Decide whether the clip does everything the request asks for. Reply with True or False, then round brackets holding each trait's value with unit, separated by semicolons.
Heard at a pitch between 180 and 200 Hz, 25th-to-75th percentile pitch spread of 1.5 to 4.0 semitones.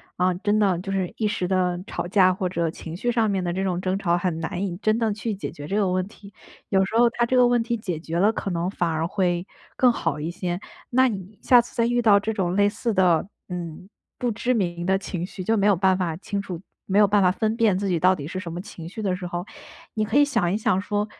True (190 Hz; 3.3 semitones)